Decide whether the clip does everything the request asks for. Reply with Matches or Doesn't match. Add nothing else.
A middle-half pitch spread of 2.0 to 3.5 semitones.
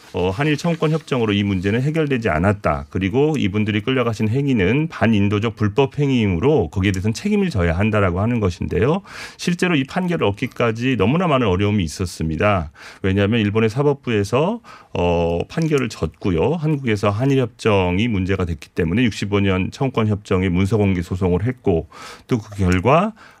Doesn't match